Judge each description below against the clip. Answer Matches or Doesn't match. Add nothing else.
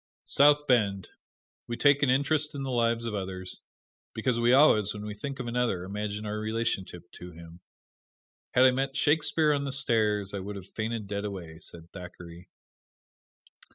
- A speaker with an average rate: Matches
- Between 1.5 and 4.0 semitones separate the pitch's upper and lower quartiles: Doesn't match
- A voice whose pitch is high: Doesn't match